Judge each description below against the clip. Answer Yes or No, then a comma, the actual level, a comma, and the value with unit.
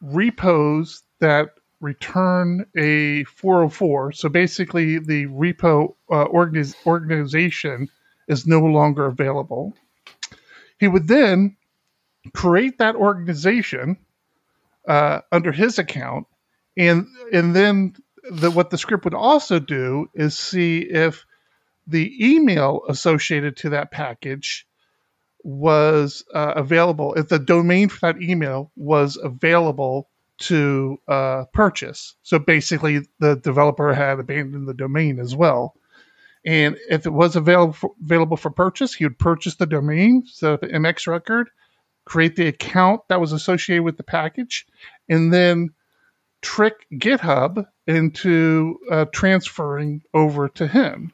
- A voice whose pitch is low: No, medium, 165 Hz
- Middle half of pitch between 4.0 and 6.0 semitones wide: No, average, 3.6 semitones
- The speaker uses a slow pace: Yes, slow, 125 wpm